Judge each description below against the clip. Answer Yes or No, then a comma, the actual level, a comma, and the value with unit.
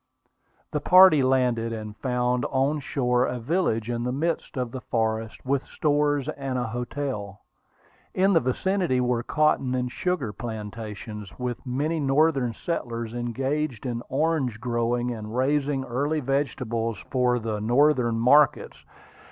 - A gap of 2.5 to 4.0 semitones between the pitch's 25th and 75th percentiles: Yes, average, 3.6 semitones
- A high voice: No, low, 125 Hz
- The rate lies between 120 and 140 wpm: Yes, slow, 135 wpm